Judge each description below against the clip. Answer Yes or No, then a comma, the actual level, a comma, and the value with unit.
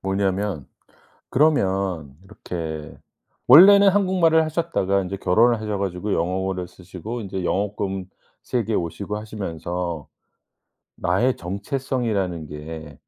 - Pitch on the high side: No, very low, 95 Hz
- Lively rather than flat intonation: No, average, 4.8 semitones